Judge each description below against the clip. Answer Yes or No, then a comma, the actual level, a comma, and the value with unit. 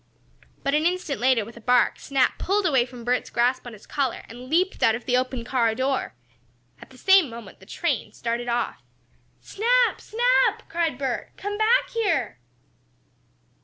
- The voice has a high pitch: Yes, very high, 260 Hz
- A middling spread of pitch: No, wide, 7.2 semitones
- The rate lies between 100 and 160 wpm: No, average, 170 wpm